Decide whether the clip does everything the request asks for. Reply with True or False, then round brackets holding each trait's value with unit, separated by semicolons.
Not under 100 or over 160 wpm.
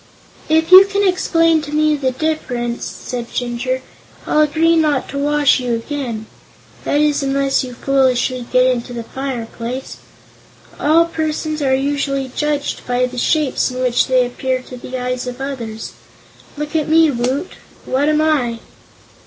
True (155 wpm)